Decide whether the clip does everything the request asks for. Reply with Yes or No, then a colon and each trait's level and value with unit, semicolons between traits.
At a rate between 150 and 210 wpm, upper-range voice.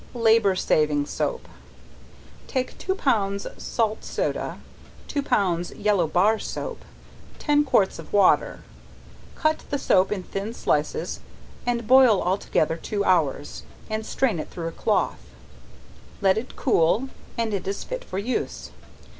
No: average, 140 wpm; high, 205 Hz